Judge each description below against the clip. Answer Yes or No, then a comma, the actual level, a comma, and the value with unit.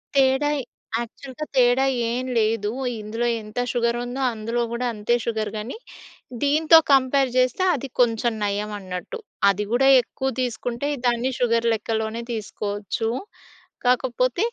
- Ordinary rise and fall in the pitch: Yes, average, 3.0 semitones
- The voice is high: Yes, high, 240 Hz